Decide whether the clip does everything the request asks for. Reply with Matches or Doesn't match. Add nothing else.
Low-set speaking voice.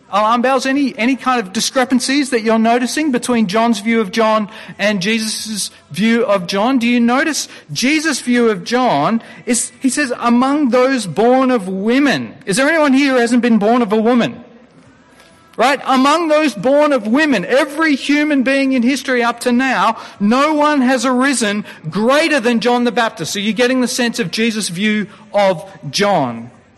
Doesn't match